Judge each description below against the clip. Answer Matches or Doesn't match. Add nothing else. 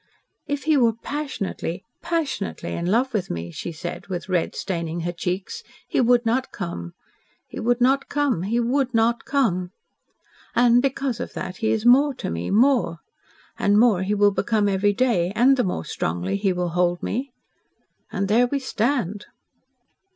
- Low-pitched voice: Doesn't match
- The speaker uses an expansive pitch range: Matches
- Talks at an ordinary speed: Matches